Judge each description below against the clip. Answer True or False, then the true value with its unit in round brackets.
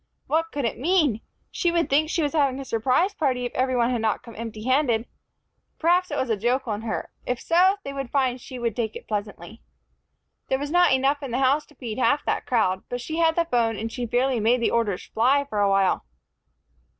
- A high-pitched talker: True (255 Hz)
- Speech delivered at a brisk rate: True (230 wpm)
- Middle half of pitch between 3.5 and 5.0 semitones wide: True (4.2 semitones)